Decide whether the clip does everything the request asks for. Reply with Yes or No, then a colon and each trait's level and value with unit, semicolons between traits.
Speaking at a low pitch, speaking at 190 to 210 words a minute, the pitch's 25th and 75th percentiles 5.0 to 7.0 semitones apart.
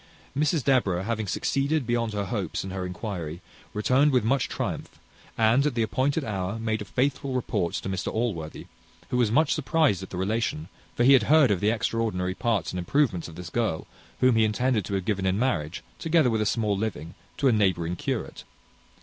Yes: low, 110 Hz; average, 200 wpm; average, 5.3 semitones